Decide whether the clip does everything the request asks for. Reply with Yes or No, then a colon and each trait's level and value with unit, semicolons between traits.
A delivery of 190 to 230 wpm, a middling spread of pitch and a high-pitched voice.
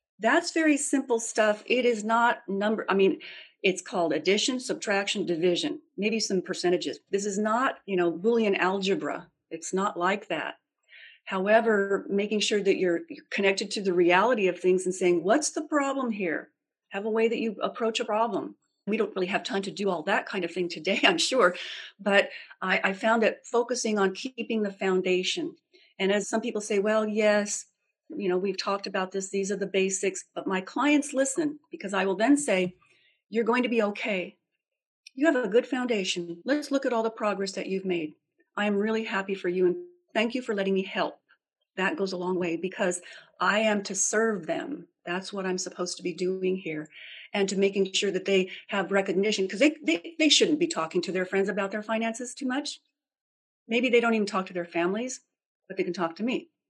Yes: fast, 205 wpm; average, 4.0 semitones; high, 205 Hz